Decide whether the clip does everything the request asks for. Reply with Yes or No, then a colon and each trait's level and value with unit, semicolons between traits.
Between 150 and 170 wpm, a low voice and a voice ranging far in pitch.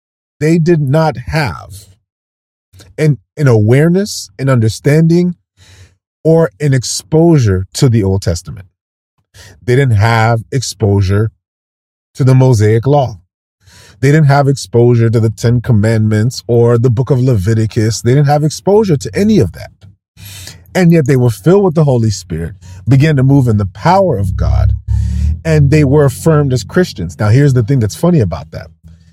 Yes: average, 155 wpm; low, 115 Hz; wide, 6.7 semitones